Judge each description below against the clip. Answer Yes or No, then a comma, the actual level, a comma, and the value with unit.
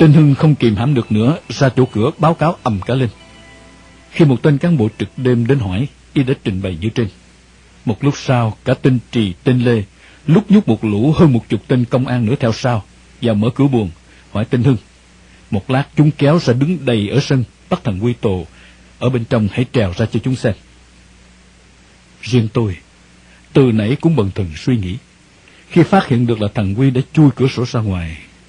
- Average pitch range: No, wide, 5.9 semitones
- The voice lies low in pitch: Yes, low, 120 Hz